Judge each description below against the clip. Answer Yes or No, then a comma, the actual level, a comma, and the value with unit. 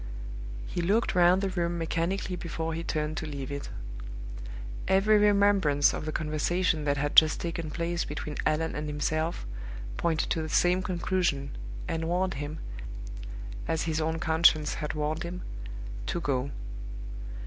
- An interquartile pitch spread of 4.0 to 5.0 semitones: No, narrow, 2.6 semitones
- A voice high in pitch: No, medium, 165 Hz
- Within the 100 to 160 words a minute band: Yes, average, 150 wpm